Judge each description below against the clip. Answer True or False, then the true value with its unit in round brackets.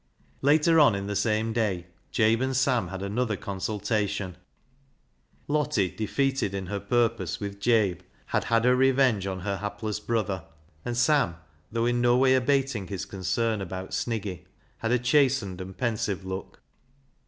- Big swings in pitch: False (4.1 semitones)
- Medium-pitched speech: False (110 Hz)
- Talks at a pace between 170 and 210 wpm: False (155 wpm)